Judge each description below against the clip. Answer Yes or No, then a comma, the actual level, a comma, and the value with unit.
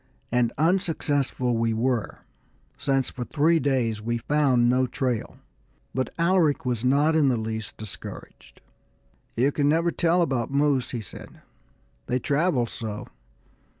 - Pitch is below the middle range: Yes, low, 130 Hz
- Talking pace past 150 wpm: No, slow, 135 wpm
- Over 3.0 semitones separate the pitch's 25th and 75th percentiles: Yes, average, 4.0 semitones